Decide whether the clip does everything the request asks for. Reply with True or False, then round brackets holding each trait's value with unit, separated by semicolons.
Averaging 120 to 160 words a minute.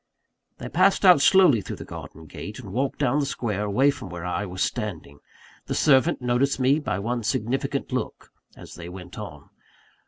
False (185 wpm)